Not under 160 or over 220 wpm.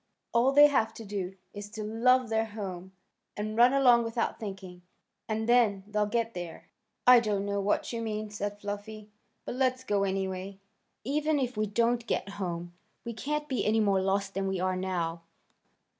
Yes: average, 180 wpm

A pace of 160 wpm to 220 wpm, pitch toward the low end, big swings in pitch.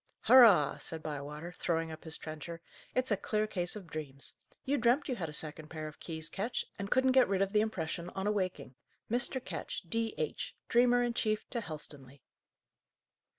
No: average, 180 wpm; medium, 185 Hz; wide, 6.6 semitones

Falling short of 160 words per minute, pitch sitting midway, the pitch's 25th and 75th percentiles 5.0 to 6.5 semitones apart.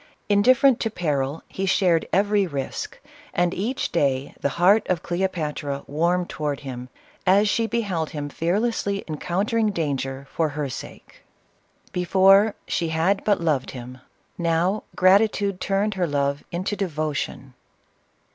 Yes: average, 145 wpm; medium, 175 Hz; average, 5.3 semitones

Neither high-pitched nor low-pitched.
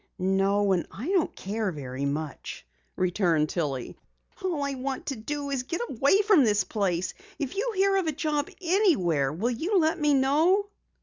No: very high, 255 Hz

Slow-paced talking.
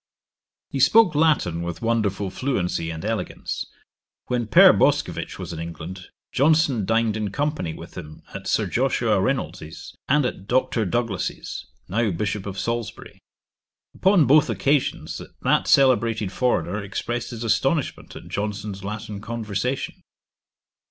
Yes: slow, 130 wpm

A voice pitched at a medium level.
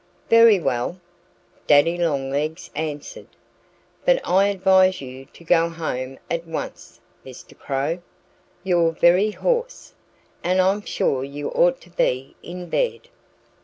Yes: medium, 170 Hz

